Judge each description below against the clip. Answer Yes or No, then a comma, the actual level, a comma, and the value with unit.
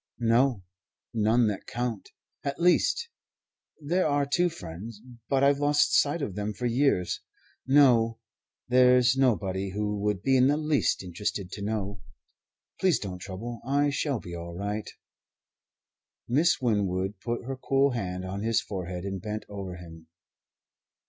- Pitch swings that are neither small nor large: No, wide, 5.7 semitones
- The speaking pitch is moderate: No, low, 115 Hz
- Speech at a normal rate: Yes, average, 145 wpm